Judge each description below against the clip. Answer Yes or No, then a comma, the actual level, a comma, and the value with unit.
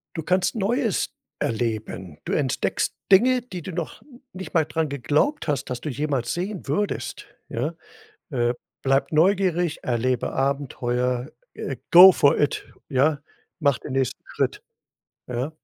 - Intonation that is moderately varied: No, wide, 6.2 semitones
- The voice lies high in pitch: No, medium, 145 Hz